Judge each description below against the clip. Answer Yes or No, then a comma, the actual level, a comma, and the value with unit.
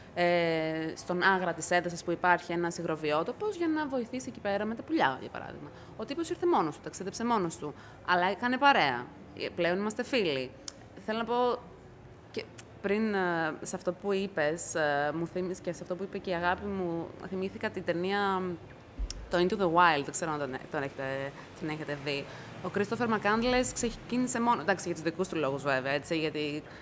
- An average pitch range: Yes, average, 4.8 semitones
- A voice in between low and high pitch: Yes, medium, 180 Hz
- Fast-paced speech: Yes, fast, 190 wpm